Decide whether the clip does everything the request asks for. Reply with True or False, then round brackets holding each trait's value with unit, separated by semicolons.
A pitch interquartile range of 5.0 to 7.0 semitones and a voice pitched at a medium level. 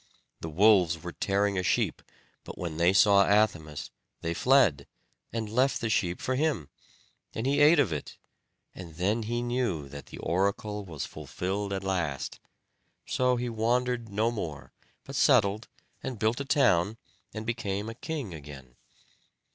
False (5.6 semitones; 105 Hz)